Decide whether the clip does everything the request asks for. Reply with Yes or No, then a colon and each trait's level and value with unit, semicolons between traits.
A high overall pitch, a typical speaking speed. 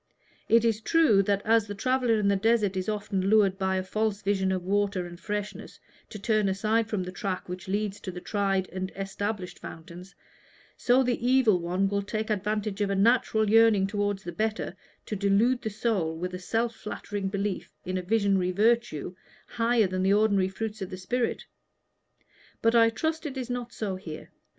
Yes: high, 205 Hz; average, 190 wpm